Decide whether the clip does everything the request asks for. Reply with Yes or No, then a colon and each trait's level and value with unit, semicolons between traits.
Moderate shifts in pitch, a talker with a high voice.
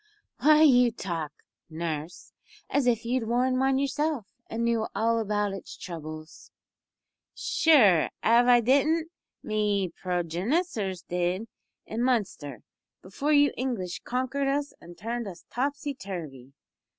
No: wide, 6.7 semitones; high, 230 Hz